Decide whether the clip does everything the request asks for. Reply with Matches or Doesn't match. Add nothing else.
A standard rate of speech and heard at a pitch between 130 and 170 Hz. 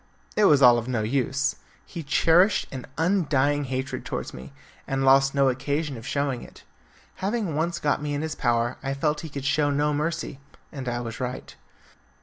Matches